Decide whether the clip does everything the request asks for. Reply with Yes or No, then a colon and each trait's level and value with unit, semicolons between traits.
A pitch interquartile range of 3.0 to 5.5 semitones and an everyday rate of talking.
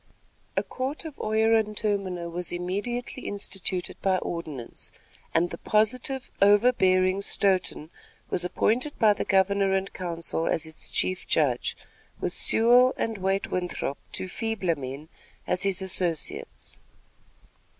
No: average, 3.6 semitones; slow, 130 wpm